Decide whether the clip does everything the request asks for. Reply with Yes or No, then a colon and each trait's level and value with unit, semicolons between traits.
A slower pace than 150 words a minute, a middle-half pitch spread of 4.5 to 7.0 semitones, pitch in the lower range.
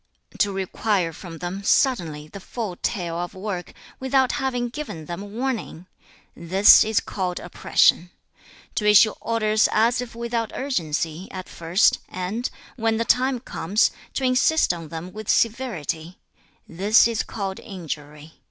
No: average, 140 wpm; average, 5.0 semitones; high, 200 Hz